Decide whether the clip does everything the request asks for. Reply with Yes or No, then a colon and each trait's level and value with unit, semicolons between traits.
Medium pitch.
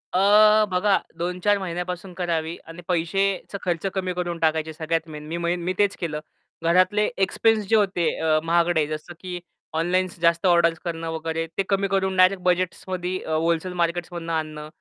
Yes: medium, 175 Hz